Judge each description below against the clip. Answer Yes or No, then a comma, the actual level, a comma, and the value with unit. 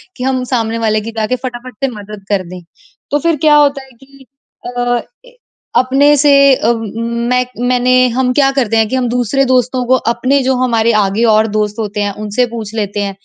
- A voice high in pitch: Yes, high, 245 Hz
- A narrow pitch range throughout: No, average, 3.0 semitones